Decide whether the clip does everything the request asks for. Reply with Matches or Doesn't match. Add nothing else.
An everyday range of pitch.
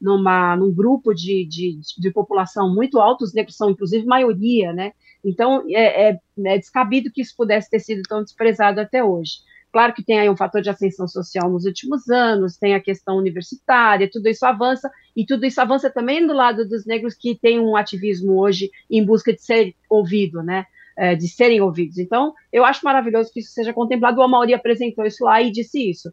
Matches